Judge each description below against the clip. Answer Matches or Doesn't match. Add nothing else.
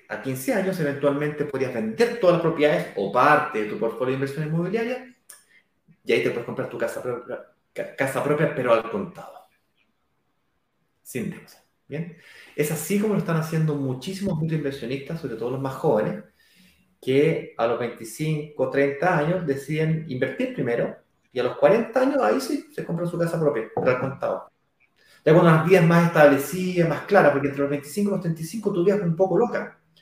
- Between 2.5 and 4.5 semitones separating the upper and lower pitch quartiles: Doesn't match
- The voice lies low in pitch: Doesn't match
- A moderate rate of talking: Matches